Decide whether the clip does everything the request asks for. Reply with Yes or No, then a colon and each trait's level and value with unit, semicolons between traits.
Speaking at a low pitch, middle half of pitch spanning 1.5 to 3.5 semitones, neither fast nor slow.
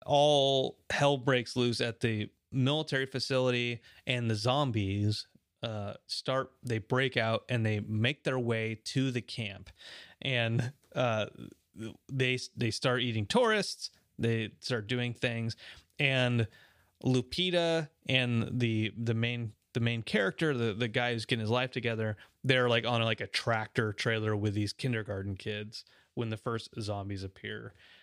Yes: low, 120 Hz; average, 2.7 semitones; average, 145 wpm